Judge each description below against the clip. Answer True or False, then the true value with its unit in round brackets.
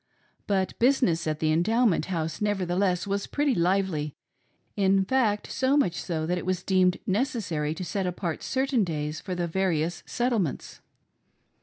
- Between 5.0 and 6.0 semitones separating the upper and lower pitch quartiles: False (3.8 semitones)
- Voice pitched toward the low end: False (185 Hz)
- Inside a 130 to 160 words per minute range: True (150 wpm)